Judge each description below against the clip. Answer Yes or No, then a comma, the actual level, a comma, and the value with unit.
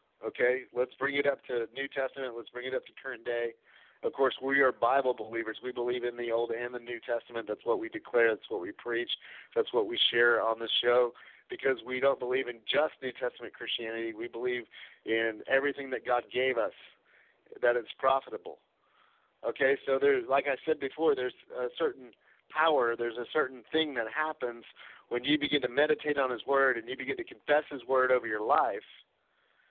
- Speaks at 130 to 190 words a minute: No, average, 200 wpm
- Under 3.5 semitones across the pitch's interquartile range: Yes, narrow, 2.5 semitones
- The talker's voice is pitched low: Yes, low, 125 Hz